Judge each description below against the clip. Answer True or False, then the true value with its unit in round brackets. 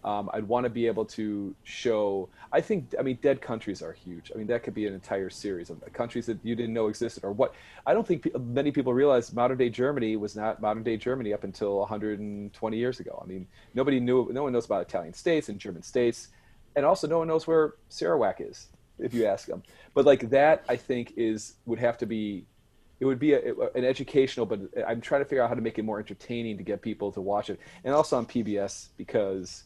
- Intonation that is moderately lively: True (3.6 semitones)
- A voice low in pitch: True (115 Hz)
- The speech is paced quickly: True (235 wpm)